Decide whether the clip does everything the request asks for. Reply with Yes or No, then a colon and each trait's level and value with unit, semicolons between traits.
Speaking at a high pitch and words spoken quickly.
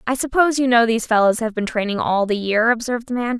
Yes: high, 235 Hz; fast, 265 wpm